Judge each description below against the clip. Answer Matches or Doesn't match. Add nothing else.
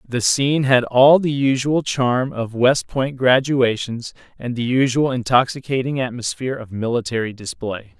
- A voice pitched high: Doesn't match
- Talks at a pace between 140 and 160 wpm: Matches